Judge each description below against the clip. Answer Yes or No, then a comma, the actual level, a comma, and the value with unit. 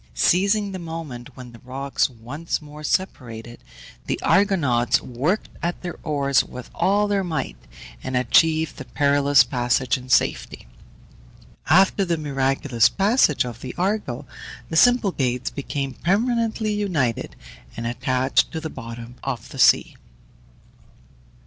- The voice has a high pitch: No, medium, 140 Hz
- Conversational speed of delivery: No, slow, 130 wpm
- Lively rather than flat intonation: Yes, wide, 6.6 semitones